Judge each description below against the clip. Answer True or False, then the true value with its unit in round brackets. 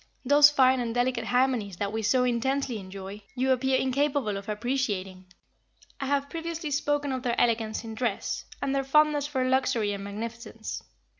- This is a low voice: False (250 Hz)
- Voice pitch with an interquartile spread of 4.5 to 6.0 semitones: False (3.8 semitones)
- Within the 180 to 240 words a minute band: False (165 wpm)